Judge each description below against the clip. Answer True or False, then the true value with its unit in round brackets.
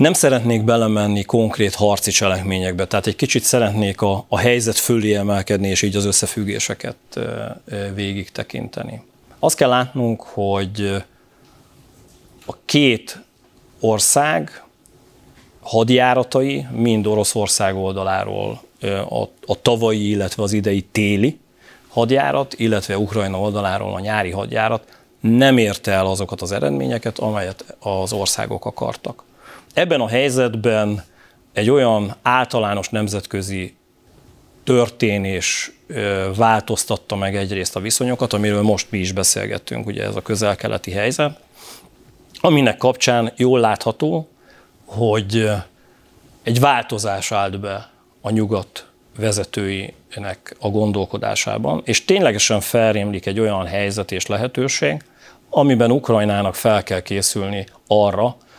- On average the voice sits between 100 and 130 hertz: True (105 Hz)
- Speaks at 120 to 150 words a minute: False (110 wpm)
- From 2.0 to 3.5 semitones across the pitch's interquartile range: True (2.9 semitones)